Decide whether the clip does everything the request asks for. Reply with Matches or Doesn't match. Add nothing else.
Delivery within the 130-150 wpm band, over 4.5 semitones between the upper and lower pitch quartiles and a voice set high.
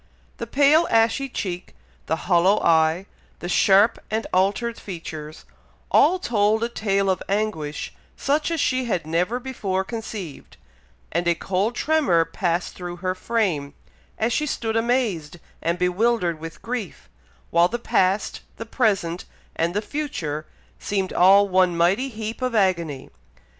Matches